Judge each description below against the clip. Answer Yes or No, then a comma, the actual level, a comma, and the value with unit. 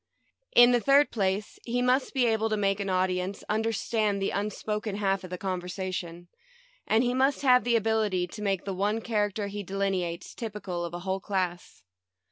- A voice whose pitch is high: Yes, high, 200 Hz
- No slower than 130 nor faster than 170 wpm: No, average, 195 wpm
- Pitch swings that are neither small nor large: Yes, average, 3.0 semitones